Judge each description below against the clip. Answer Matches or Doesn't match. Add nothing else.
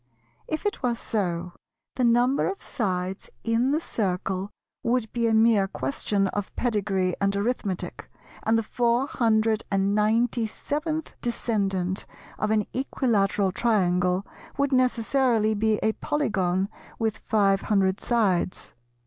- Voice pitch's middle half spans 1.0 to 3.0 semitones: Doesn't match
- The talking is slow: Matches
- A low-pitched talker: Doesn't match